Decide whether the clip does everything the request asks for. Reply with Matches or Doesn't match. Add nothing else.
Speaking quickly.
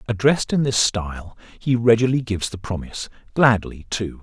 Doesn't match